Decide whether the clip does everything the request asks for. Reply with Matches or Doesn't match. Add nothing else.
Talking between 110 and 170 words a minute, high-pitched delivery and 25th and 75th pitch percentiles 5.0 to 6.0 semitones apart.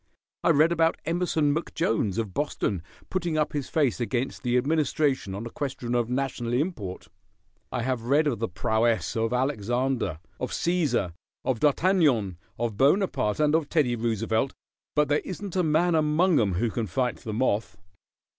Doesn't match